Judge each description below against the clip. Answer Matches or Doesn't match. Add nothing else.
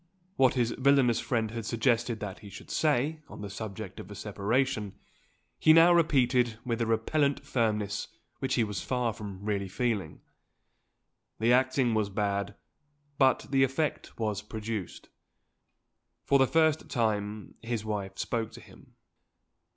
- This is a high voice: Doesn't match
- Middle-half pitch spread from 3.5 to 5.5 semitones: Matches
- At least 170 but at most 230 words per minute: Doesn't match